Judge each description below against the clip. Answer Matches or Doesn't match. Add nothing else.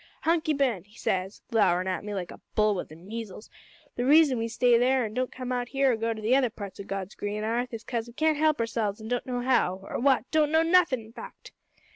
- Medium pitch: Doesn't match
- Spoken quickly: Matches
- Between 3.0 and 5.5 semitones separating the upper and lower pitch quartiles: Matches